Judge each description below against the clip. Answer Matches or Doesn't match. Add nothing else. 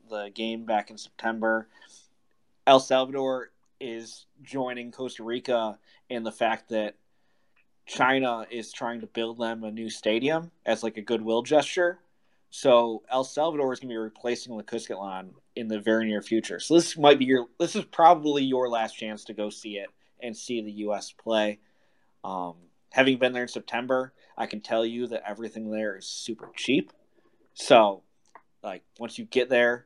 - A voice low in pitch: Matches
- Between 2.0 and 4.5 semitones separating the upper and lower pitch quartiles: Matches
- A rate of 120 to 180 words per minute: Matches